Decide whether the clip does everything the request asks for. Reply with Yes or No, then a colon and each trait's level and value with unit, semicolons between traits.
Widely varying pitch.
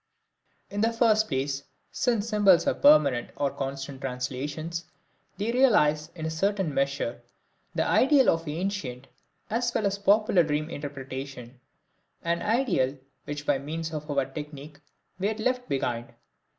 Yes: wide, 7.0 semitones